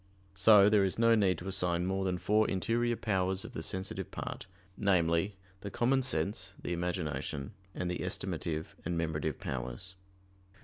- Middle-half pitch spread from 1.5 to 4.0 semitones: Yes, average, 3.2 semitones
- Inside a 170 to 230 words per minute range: No, average, 160 wpm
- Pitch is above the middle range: No, very low, 95 Hz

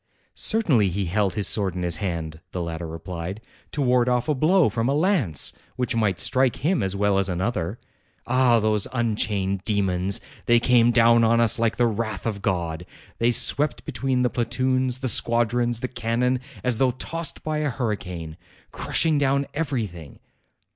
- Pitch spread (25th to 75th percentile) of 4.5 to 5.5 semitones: Yes, average, 4.8 semitones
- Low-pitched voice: Yes, low, 115 Hz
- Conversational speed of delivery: Yes, average, 170 wpm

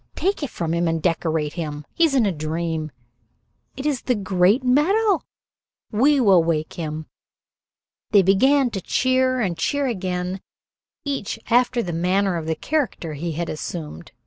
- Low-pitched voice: No, high, 190 Hz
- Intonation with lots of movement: Yes, wide, 7.8 semitones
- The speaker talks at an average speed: Yes, average, 160 wpm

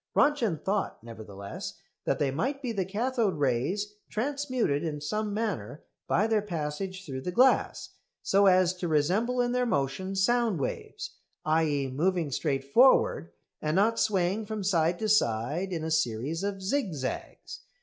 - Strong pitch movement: Yes, wide, 6.5 semitones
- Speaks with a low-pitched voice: No, medium, 185 Hz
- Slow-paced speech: No, average, 155 wpm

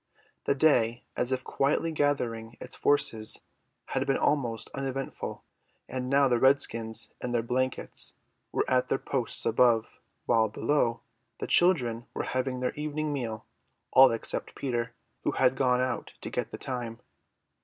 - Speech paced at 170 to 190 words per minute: No, average, 150 wpm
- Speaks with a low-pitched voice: Yes, low, 125 Hz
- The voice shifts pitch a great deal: No, average, 2.8 semitones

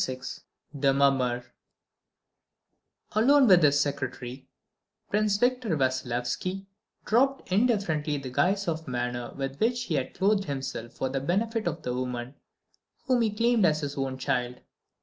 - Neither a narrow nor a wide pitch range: No, wide, 8.1 semitones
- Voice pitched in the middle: Yes, medium, 145 Hz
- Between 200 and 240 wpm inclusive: No, average, 140 wpm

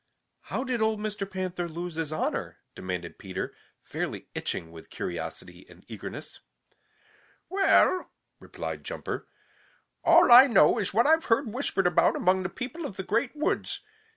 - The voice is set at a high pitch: Yes, high, 205 Hz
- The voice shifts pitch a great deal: Yes, wide, 6.5 semitones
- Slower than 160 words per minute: Yes, average, 150 wpm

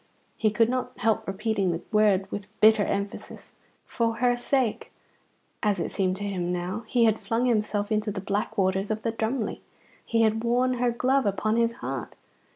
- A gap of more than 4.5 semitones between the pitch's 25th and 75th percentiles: No, average, 2.7 semitones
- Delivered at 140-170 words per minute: No, average, 180 wpm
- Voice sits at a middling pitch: No, high, 215 Hz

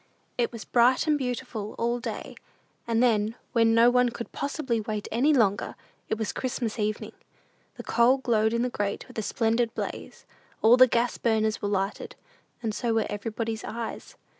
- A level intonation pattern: Yes, narrow, 2.0 semitones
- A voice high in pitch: Yes, high, 230 Hz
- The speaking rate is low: No, average, 175 wpm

